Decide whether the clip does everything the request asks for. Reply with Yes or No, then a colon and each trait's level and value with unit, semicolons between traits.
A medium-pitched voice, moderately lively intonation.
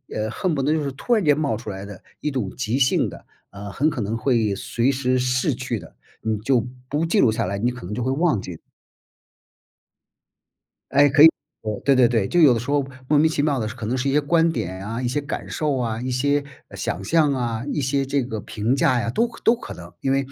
No: low, 130 Hz; average, 4.3 semitones